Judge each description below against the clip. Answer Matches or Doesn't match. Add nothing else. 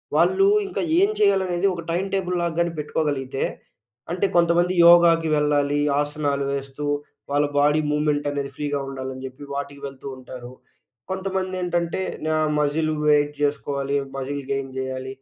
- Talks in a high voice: Doesn't match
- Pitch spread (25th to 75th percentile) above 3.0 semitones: Matches